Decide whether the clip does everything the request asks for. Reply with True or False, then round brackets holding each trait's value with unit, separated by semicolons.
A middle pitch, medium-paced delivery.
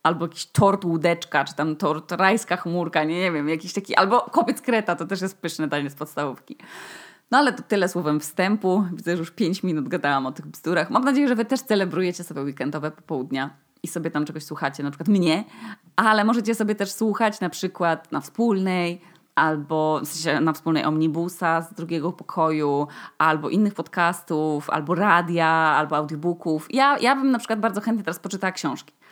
False (170 Hz; 190 wpm)